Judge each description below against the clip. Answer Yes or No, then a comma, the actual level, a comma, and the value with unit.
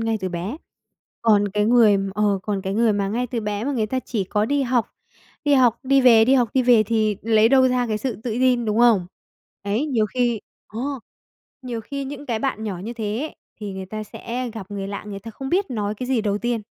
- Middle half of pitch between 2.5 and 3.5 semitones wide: Yes, average, 3.2 semitones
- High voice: Yes, high, 225 Hz